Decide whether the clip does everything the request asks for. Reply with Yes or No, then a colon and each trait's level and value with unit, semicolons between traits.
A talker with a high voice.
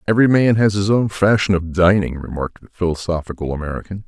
No: very low, 95 Hz